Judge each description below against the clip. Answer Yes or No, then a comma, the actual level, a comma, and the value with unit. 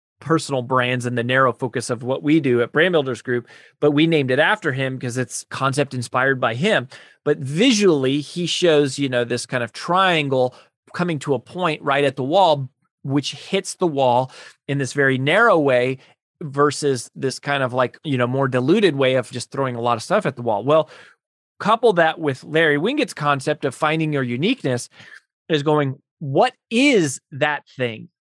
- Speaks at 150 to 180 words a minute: No, average, 190 wpm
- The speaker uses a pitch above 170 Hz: No, medium, 140 Hz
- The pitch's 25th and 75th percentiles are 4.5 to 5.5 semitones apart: No, average, 3.4 semitones